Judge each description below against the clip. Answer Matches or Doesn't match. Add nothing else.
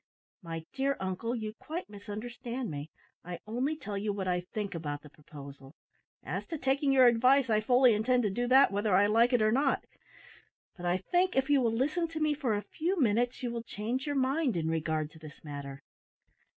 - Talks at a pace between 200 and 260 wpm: Matches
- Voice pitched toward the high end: Matches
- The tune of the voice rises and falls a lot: Matches